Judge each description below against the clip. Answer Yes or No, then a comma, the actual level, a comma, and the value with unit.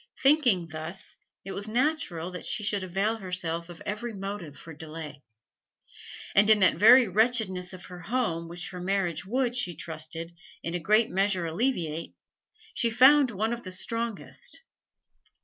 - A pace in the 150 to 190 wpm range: Yes, average, 155 wpm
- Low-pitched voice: No, high, 190 Hz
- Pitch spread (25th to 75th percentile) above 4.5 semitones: Yes, average, 5.1 semitones